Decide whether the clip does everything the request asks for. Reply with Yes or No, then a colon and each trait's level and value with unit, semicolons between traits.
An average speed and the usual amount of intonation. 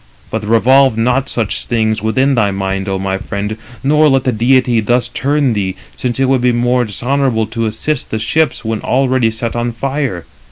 Yes: average, 195 wpm; average, 3.3 semitones